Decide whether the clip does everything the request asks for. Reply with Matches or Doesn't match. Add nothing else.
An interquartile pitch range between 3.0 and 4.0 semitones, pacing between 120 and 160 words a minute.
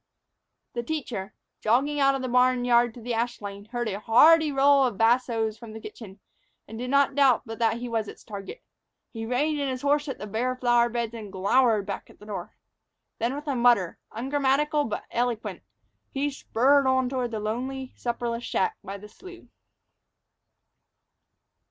Doesn't match